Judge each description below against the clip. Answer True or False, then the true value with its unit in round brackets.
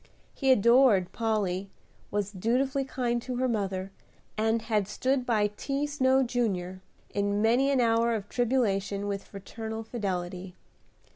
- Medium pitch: False (225 Hz)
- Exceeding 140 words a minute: False (135 wpm)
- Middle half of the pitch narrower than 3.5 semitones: False (4.0 semitones)